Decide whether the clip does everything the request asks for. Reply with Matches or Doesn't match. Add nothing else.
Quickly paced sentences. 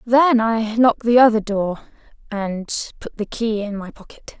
Doesn't match